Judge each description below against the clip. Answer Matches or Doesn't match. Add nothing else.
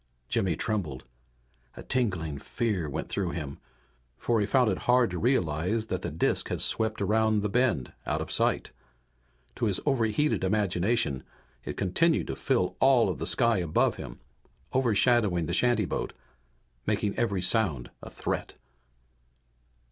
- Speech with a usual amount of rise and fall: Matches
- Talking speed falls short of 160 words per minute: Matches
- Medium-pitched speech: Doesn't match